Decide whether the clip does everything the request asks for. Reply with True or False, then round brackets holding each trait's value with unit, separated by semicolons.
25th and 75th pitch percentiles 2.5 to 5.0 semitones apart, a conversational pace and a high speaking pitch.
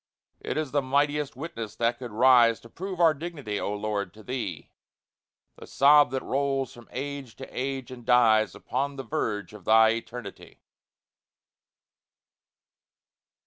False (3.9 semitones; 145 wpm; 125 Hz)